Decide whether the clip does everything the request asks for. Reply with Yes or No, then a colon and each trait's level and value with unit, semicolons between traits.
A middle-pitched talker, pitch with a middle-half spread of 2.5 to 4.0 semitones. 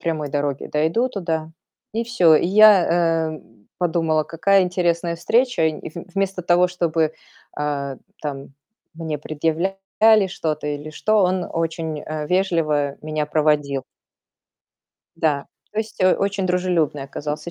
Yes: medium, 165 Hz; average, 3.2 semitones